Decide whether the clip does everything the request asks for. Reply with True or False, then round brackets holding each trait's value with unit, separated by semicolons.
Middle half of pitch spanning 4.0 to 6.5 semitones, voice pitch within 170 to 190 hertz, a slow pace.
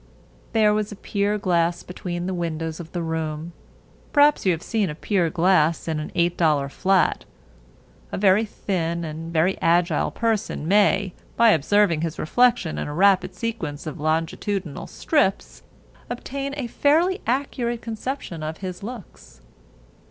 False (4.8 semitones; 185 Hz; 145 wpm)